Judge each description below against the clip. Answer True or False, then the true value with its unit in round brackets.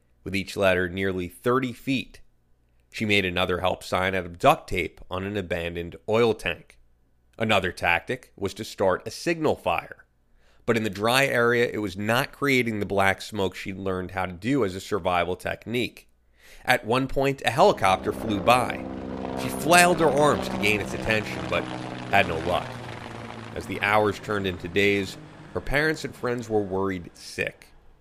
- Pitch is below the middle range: True (95 Hz)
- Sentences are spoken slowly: False (175 wpm)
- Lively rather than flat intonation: True (5.7 semitones)